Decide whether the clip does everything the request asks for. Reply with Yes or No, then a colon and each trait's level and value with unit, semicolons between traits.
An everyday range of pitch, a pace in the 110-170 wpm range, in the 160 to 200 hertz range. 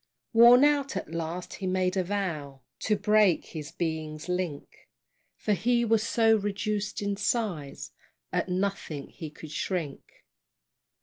Yes: average, 4.9 semitones; slow, 135 wpm; high, 190 Hz